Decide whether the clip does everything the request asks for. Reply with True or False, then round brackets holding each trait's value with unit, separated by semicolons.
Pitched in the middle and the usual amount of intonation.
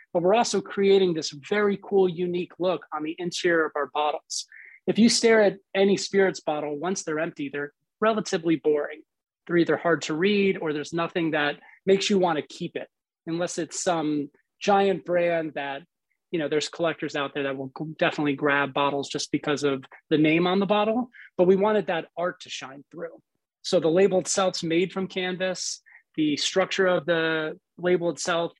True (175 Hz; 3.8 semitones)